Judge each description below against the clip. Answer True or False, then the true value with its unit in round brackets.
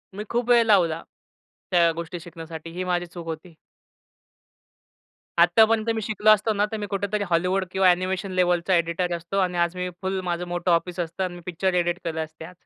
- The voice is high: False (180 Hz)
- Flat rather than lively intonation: True (2.2 semitones)